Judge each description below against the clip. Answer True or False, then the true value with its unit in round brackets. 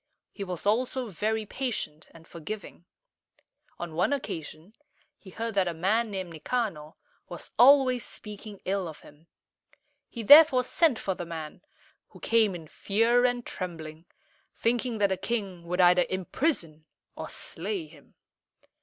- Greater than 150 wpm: False (145 wpm)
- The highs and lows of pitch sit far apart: True (5.7 semitones)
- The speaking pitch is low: False (200 Hz)